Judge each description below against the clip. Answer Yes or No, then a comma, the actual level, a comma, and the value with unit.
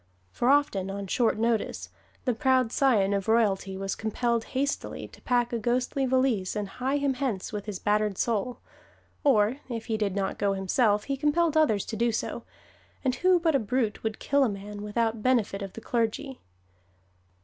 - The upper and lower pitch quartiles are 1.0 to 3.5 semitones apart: No, average, 4.0 semitones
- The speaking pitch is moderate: No, high, 230 Hz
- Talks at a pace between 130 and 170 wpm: No, average, 180 wpm